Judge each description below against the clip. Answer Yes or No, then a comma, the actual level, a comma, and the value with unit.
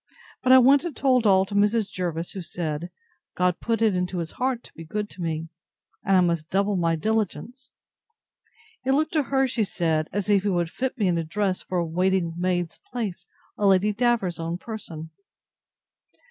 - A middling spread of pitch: Yes, average, 4.6 semitones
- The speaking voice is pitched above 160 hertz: Yes, high, 190 Hz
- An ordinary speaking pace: Yes, average, 190 wpm